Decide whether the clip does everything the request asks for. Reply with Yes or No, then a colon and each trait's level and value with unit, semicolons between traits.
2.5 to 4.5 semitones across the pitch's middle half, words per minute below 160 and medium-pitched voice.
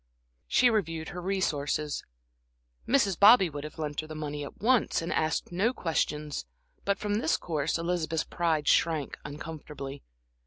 Yes: average, 4.1 semitones; average, 150 wpm; medium, 160 Hz